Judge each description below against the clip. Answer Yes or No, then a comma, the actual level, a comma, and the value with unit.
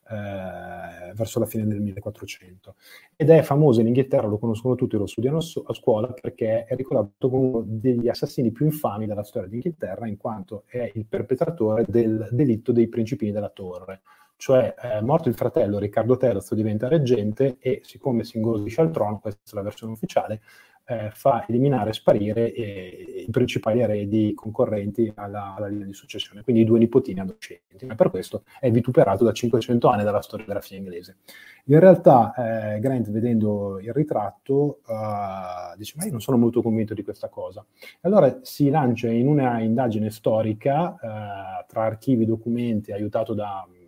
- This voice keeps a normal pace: No, fast, 175 wpm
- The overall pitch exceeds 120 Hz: No, low, 115 Hz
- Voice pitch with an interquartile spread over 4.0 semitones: No, average, 3.2 semitones